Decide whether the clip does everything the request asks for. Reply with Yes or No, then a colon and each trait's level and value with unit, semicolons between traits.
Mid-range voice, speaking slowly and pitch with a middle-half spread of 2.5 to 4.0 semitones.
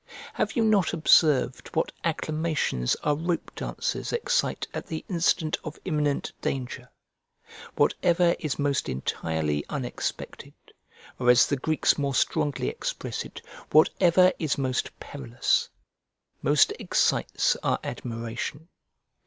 No: medium, 150 Hz; slow, 115 wpm; average, 4.7 semitones